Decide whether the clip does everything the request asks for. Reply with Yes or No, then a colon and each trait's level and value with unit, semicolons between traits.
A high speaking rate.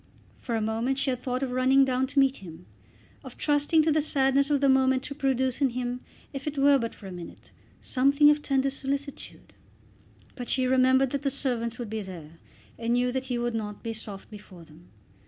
Yes: fast, 210 wpm